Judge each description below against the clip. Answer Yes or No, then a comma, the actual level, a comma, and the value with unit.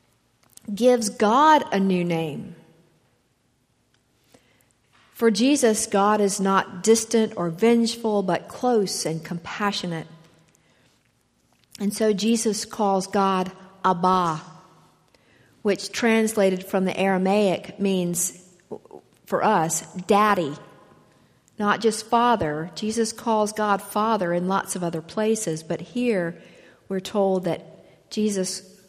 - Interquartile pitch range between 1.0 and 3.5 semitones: Yes, average, 3.2 semitones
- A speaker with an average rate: No, slow, 105 wpm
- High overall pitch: Yes, high, 195 Hz